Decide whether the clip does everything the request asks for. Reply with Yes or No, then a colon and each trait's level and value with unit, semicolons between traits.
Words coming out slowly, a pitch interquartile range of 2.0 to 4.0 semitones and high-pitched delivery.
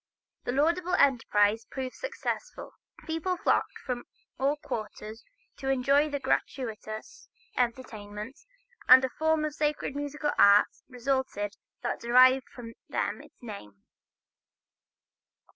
No: slow, 110 wpm; average, 4.5 semitones; very high, 260 Hz